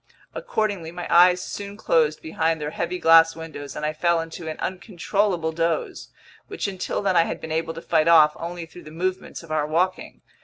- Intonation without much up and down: Yes, narrow, 2.2 semitones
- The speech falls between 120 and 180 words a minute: No, average, 195 wpm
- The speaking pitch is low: No, medium, 165 Hz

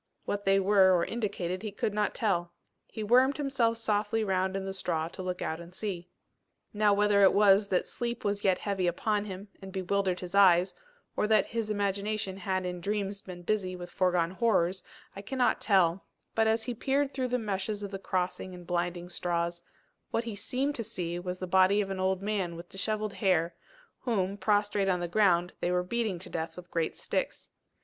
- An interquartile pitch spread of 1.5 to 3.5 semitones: Yes, average, 2.8 semitones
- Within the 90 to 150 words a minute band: No, average, 200 wpm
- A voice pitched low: No, high, 195 Hz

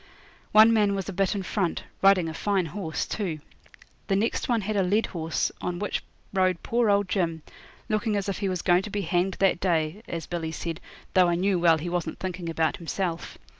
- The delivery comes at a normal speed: No, fast, 210 wpm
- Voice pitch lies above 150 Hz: Yes, medium, 185 Hz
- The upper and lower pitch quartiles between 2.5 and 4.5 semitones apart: Yes, average, 3.0 semitones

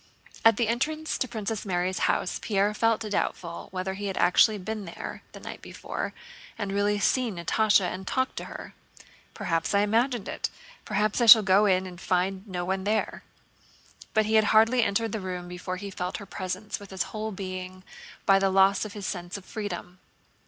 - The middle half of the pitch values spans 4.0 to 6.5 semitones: No, average, 2.7 semitones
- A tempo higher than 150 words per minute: Yes, average, 190 wpm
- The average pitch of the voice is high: Yes, high, 200 Hz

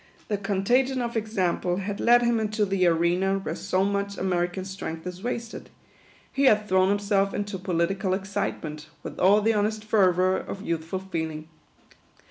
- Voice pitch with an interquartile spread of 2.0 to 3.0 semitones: Yes, narrow, 2.6 semitones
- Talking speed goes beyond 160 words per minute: No, average, 155 wpm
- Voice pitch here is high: Yes, high, 195 Hz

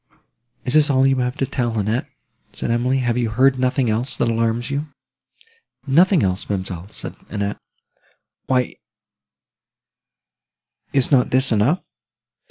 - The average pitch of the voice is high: No, low, 125 Hz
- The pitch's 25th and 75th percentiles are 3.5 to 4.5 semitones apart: No, average, 3.1 semitones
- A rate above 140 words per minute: No, slow, 135 wpm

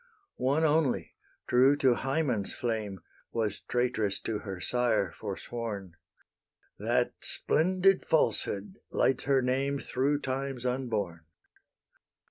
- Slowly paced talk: Yes, slow, 100 wpm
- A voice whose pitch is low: Yes, low, 125 Hz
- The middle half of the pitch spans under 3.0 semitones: No, average, 4.2 semitones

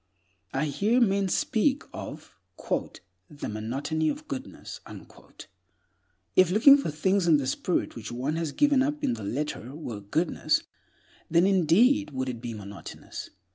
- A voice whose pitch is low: No, medium, 160 Hz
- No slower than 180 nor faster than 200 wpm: No, average, 140 wpm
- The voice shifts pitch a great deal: Yes, wide, 8.0 semitones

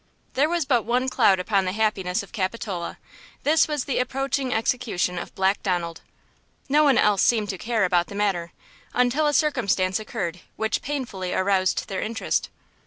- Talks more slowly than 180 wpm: Yes, average, 170 wpm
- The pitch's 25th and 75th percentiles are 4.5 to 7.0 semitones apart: Yes, average, 5.3 semitones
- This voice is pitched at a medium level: No, high, 215 Hz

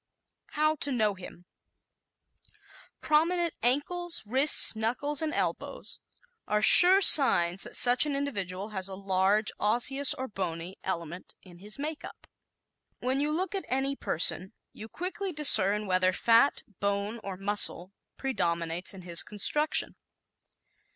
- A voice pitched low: No, high, 220 Hz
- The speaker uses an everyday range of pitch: No, wide, 7.2 semitones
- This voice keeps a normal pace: No, slow, 130 wpm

